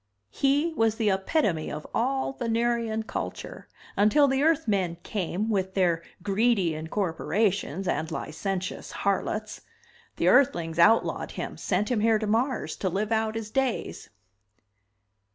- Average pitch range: Yes, average, 3.7 semitones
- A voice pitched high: Yes, high, 215 Hz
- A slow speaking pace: Yes, slow, 130 wpm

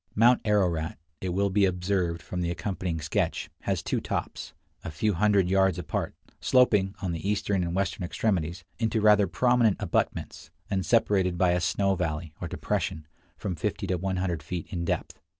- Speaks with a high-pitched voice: No, very low, 95 Hz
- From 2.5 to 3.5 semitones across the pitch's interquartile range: Yes, average, 2.8 semitones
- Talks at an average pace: Yes, average, 170 wpm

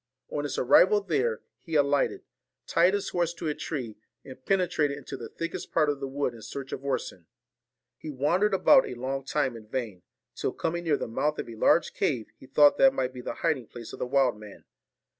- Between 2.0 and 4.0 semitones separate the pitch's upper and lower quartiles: No, average, 4.6 semitones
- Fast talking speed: Yes, fast, 215 wpm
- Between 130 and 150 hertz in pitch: Yes, medium, 140 Hz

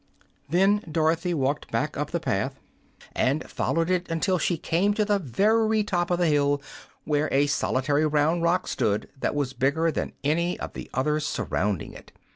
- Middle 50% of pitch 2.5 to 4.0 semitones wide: Yes, average, 3.7 semitones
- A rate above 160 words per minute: Yes, average, 175 wpm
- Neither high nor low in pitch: Yes, medium, 160 Hz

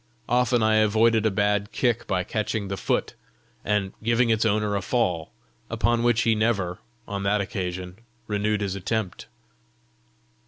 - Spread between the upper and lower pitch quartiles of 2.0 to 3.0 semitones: Yes, narrow, 2.4 semitones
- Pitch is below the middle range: Yes, low, 105 Hz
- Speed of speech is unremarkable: Yes, average, 150 wpm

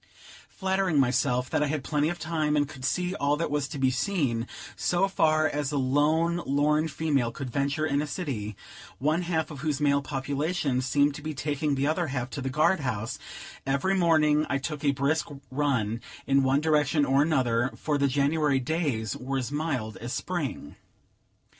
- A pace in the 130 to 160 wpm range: No, average, 185 wpm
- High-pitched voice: No, medium, 145 Hz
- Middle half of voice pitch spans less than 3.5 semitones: Yes, average, 2.8 semitones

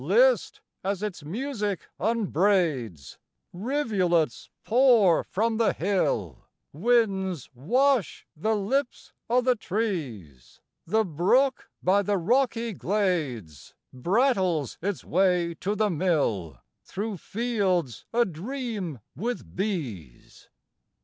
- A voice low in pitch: No, high, 195 Hz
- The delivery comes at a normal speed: No, slow, 95 wpm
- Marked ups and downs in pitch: Yes, wide, 6.1 semitones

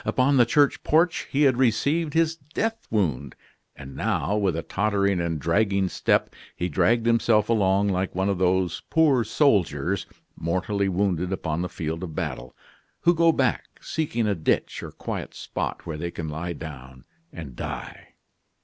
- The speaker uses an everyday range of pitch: No, wide, 6.4 semitones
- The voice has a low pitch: Yes, low, 100 Hz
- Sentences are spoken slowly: No, average, 165 wpm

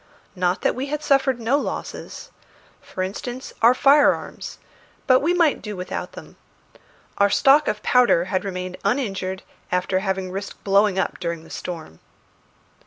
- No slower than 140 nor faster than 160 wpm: Yes, average, 150 wpm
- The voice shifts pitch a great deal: Yes, wide, 5.8 semitones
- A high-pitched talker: Yes, high, 200 Hz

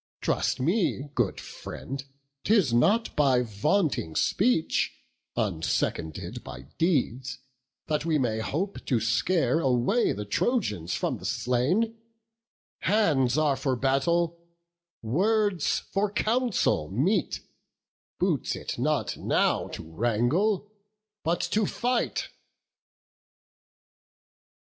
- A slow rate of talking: Yes, slow, 100 wpm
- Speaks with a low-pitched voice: No, medium, 150 Hz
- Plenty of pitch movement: Yes, wide, 8.6 semitones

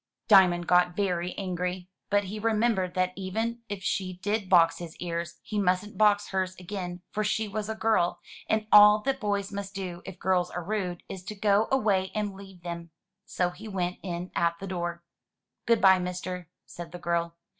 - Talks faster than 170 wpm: Yes, average, 190 wpm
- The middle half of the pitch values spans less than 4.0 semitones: Yes, average, 2.7 semitones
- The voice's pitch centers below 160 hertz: No, medium, 185 Hz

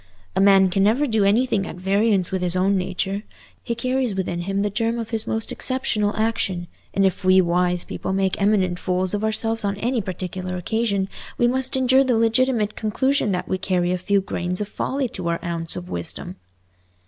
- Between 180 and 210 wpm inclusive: Yes, average, 195 wpm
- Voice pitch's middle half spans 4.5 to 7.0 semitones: No, average, 3.6 semitones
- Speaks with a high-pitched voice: Yes, high, 200 Hz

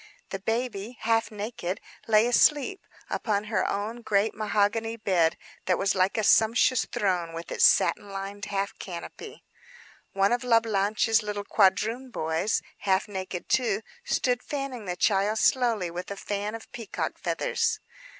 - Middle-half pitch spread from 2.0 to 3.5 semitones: Yes, average, 2.8 semitones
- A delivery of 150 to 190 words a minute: No, average, 140 wpm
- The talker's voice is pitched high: Yes, high, 210 Hz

